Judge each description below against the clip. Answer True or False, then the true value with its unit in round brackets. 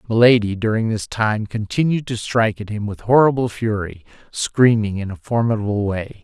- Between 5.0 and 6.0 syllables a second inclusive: True (5.2 syllables/s)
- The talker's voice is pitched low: True (110 Hz)